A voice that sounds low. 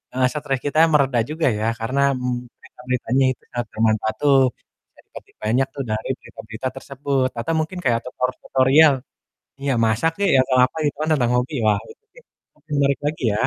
Yes: low, 130 Hz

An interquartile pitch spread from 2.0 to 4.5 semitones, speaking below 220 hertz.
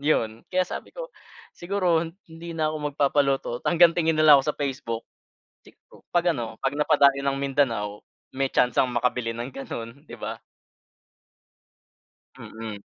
No: average, 4.9 semitones; medium, 140 Hz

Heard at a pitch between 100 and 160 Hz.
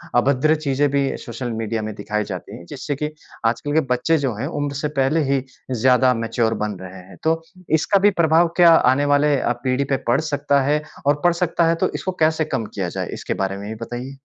Yes: low, 135 Hz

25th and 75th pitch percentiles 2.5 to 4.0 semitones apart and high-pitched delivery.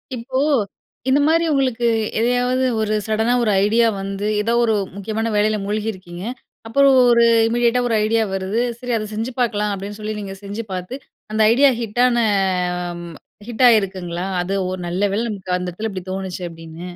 Yes: average, 3.6 semitones; high, 215 Hz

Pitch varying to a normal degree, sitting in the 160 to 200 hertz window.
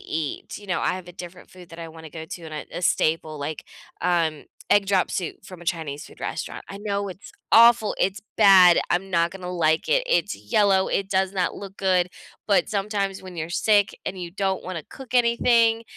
Yes: average, 3.0 semitones; medium, 185 Hz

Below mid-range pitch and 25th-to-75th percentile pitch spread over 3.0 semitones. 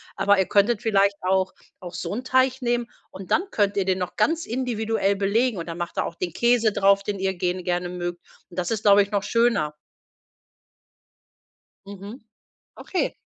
No: high, 200 Hz; average, 3.8 semitones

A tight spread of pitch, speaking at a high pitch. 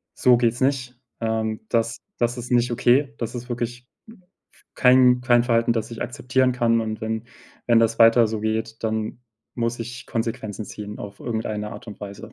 No: narrow, 1.7 semitones; low, 115 Hz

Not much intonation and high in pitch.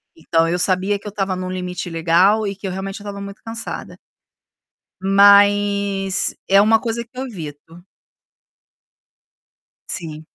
Yes: narrow, 2.2 semitones; high, 195 Hz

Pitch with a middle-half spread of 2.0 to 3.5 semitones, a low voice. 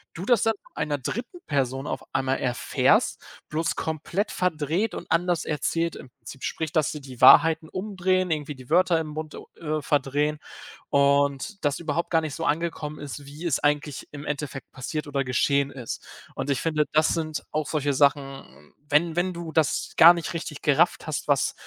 No: average, 2.8 semitones; medium, 150 Hz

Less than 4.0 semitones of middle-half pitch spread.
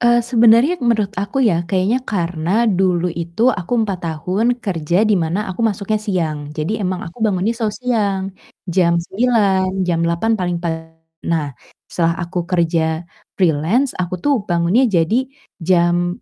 No: average, 4.6 semitones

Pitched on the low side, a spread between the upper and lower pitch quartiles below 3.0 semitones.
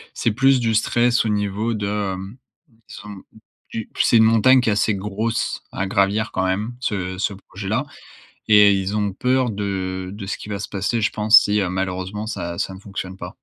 Yes: low, 105 Hz; narrow, 2.5 semitones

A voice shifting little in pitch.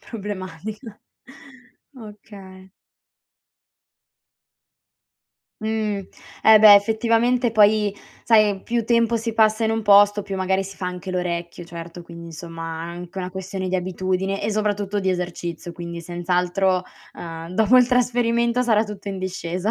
No: average, 3.3 semitones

